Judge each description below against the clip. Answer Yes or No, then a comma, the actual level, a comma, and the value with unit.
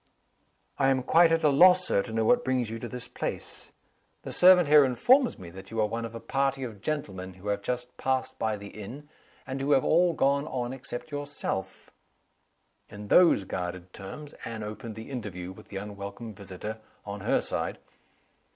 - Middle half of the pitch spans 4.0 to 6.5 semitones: Yes, wide, 5.6 semitones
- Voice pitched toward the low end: Yes, low, 120 Hz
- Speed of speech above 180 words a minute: Yes, average, 190 wpm